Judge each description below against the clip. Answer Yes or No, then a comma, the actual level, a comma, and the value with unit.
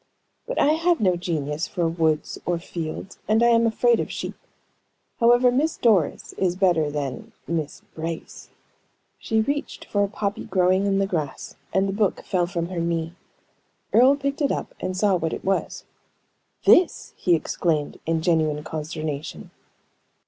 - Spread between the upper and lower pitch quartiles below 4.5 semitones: No, average, 5.3 semitones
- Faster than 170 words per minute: No, average, 160 wpm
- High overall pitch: No, medium, 180 Hz